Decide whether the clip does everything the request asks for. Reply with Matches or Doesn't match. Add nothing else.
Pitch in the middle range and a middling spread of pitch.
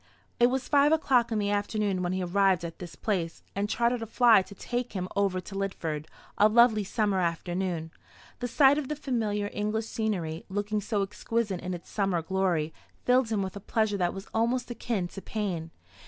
Doesn't match